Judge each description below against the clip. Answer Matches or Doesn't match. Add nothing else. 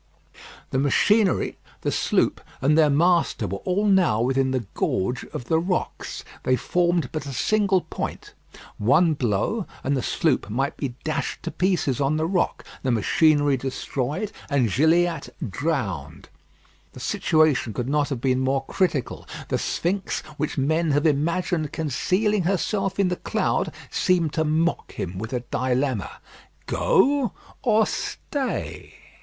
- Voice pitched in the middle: Matches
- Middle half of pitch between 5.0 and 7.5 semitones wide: Matches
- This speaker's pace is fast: Doesn't match